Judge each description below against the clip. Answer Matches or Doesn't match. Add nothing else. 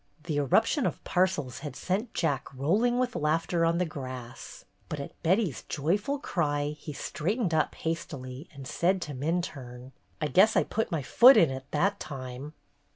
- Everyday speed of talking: Matches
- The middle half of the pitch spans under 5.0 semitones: Doesn't match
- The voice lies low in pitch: Doesn't match